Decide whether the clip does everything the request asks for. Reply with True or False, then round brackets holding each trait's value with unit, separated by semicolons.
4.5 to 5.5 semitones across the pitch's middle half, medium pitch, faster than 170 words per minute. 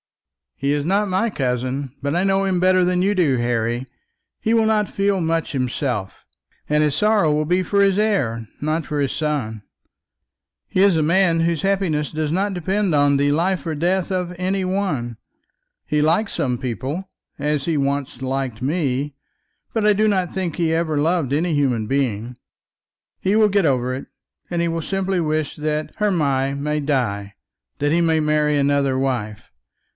True (5.2 semitones; 155 Hz; 180 wpm)